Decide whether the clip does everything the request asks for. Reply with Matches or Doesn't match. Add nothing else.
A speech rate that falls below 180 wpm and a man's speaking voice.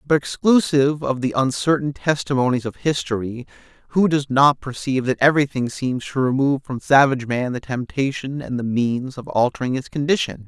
Matches